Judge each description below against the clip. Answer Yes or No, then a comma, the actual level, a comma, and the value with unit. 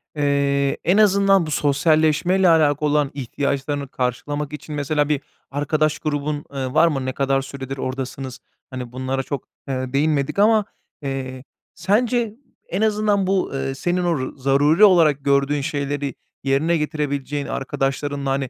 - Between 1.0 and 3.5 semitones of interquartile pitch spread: Yes, average, 2.7 semitones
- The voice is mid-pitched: Yes, medium, 145 Hz